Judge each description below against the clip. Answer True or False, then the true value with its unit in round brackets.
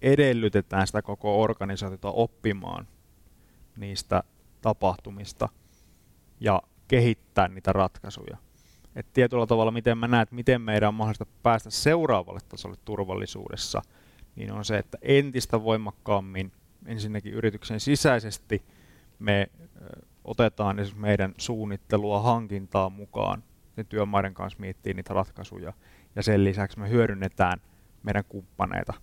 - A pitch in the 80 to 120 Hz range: True (105 Hz)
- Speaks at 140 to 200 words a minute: False (110 wpm)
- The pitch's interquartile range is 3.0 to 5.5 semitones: False (2.6 semitones)